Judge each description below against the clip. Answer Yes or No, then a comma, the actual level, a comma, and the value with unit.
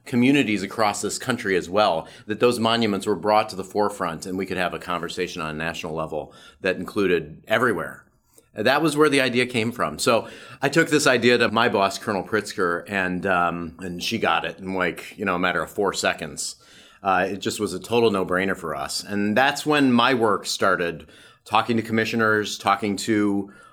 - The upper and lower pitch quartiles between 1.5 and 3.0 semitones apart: No, average, 3.8 semitones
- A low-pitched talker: Yes, low, 105 Hz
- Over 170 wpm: Yes, average, 200 wpm